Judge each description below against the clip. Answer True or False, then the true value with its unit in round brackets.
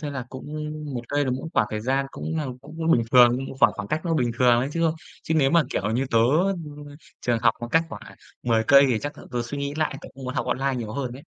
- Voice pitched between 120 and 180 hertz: True (135 Hz)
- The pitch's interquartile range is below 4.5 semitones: True (3.8 semitones)